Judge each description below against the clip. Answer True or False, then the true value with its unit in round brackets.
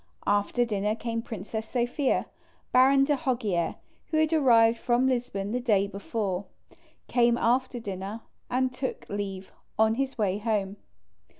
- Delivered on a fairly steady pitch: False (3.7 semitones)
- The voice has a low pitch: False (230 Hz)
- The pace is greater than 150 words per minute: False (135 wpm)